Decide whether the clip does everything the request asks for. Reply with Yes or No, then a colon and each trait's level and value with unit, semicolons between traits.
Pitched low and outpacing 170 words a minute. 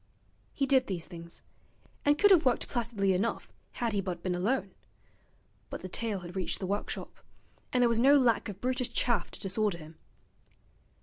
No: high, 210 Hz; average, 180 wpm